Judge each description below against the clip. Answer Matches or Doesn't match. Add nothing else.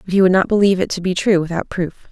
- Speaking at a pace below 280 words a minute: Doesn't match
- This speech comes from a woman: Matches